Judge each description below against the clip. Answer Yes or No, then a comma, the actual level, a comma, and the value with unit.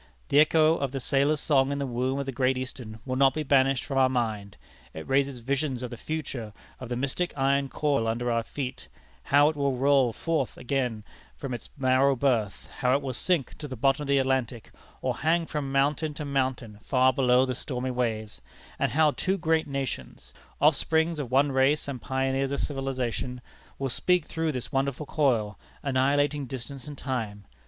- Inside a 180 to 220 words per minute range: Yes, average, 190 wpm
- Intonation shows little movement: Yes, narrow, 2.2 semitones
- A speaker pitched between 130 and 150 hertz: Yes, low, 135 Hz